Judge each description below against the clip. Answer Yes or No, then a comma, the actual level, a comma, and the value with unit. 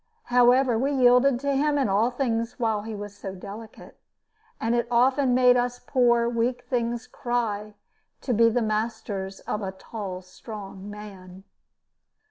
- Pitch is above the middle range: Yes, high, 230 Hz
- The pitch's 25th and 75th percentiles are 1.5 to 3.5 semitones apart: Yes, average, 3.1 semitones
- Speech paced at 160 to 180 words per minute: No, average, 150 wpm